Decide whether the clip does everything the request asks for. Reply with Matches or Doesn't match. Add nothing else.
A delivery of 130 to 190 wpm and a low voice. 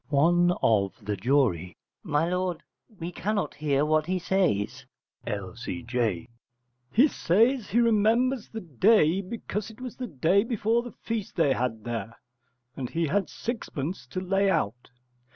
Doesn't match